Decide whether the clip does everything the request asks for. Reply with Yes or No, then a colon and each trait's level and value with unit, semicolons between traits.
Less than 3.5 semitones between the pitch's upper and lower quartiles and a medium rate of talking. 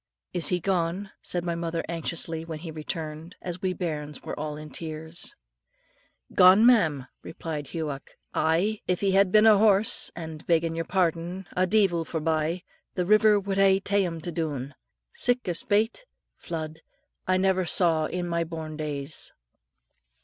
Yes: average, 3.0 semitones; average, 155 wpm